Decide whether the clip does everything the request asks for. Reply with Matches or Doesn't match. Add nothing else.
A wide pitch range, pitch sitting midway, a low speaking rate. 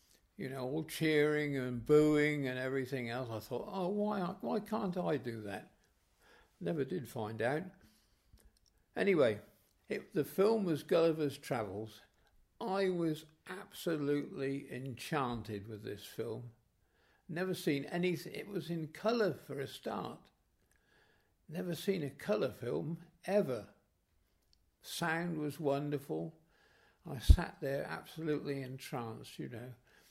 Matches